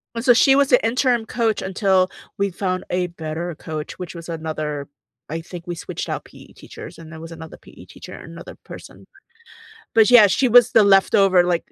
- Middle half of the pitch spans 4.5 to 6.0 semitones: Yes, average, 5.2 semitones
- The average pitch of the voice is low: No, medium, 185 Hz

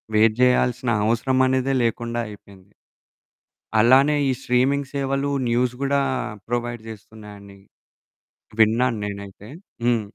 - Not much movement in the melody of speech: No, average, 3.3 semitones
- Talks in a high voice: No, low, 120 Hz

